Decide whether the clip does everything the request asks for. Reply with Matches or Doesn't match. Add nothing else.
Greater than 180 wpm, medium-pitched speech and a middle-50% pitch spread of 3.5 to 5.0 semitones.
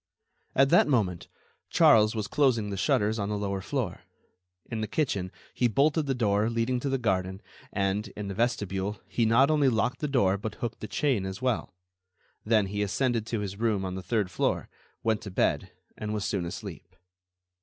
Doesn't match